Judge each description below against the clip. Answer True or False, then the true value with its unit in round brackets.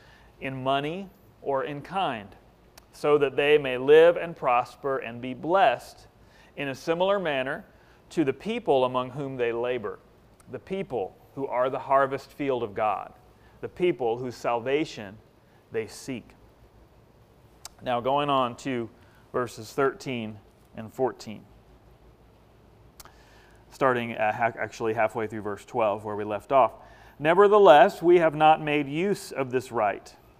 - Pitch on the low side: True (130 Hz)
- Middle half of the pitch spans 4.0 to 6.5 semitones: True (4.7 semitones)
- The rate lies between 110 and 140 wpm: True (135 wpm)